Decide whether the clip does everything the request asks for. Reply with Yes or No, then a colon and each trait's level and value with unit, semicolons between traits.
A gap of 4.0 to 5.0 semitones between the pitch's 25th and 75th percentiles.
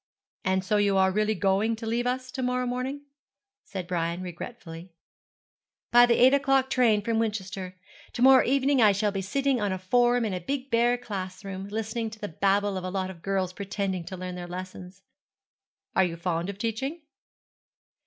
Yes: average, 4.5 semitones